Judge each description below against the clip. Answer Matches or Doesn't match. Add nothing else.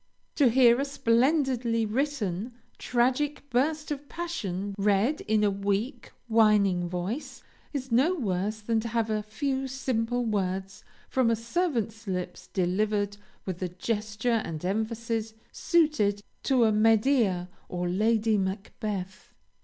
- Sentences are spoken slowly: Matches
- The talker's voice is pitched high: Matches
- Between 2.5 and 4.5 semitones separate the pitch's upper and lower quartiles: Matches